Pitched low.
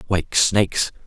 Yes: very low, 90 Hz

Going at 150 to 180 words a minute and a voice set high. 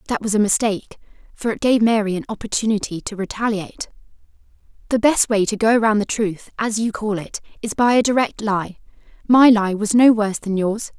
No: average, 195 wpm; high, 215 Hz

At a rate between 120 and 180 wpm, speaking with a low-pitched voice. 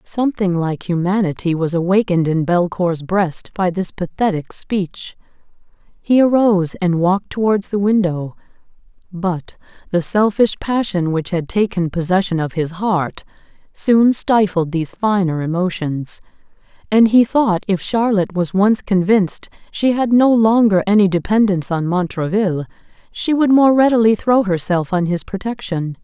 No: average, 140 wpm; high, 190 Hz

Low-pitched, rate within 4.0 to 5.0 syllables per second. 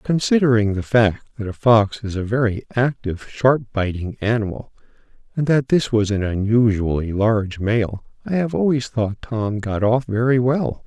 Yes: low, 115 Hz; 4.7 syllables/s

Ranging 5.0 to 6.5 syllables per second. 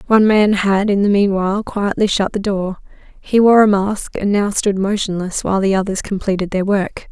Yes: 5.2 syllables/s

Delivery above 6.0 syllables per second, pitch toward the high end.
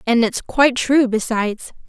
No: 4.9 syllables/s; high, 240 Hz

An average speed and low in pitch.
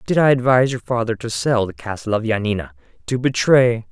Yes: average, 185 wpm; low, 120 Hz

